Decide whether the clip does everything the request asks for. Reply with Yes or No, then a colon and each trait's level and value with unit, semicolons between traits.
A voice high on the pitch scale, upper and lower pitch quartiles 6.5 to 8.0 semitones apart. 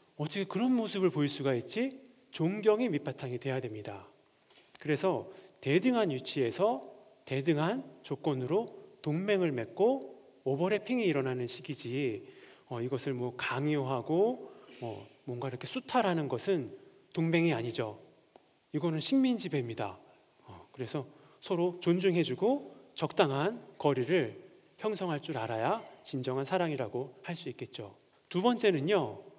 No: medium, 160 Hz; wide, 6.9 semitones